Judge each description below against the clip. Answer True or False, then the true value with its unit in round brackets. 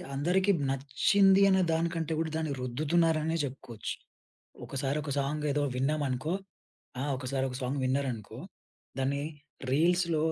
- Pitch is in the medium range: True (145 Hz)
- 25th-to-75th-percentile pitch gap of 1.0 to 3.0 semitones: False (3.7 semitones)